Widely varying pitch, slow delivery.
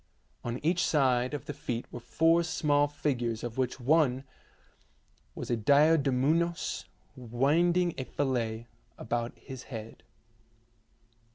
No: average, 4.4 semitones; slow, 115 wpm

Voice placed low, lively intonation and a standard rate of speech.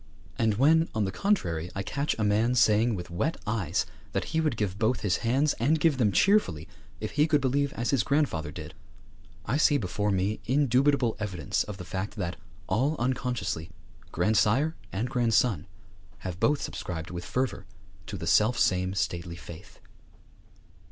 Yes: low, 110 Hz; wide, 6.4 semitones; average, 165 wpm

